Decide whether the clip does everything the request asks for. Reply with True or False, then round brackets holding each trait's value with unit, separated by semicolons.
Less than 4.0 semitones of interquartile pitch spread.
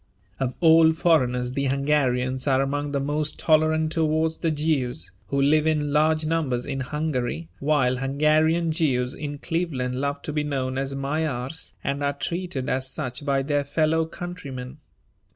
True (3.1 semitones)